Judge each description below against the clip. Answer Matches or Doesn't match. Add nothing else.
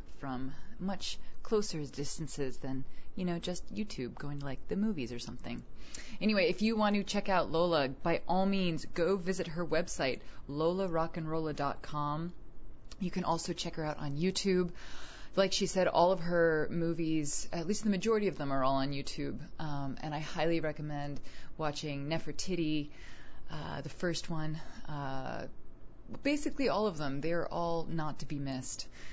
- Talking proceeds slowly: Doesn't match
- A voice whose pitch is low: Doesn't match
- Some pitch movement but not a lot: Matches